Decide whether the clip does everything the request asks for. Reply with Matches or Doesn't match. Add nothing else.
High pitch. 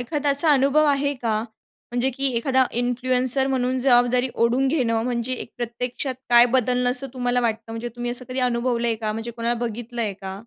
Matches